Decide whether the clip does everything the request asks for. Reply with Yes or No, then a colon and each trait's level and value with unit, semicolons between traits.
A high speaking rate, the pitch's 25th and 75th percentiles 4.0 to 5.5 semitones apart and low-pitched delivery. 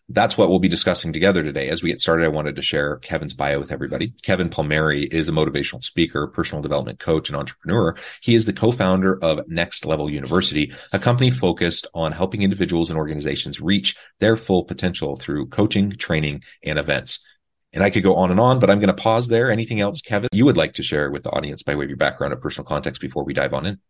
Yes: fast, 235 wpm; average, 4.5 semitones; very low, 95 Hz